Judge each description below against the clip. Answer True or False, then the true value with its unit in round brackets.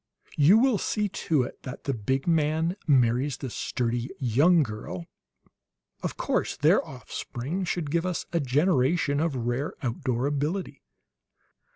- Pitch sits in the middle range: True (145 Hz)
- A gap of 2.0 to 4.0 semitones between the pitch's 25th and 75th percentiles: False (4.9 semitones)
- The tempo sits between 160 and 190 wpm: False (140 wpm)